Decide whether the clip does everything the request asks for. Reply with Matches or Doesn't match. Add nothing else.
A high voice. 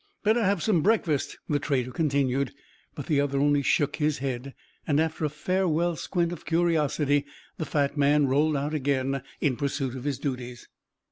Doesn't match